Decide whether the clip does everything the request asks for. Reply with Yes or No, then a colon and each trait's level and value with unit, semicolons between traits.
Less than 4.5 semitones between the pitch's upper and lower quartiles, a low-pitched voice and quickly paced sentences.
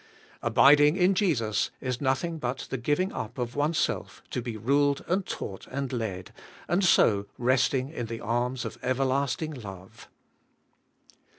No: average, 3.9 semitones; low, 130 Hz; average, 140 wpm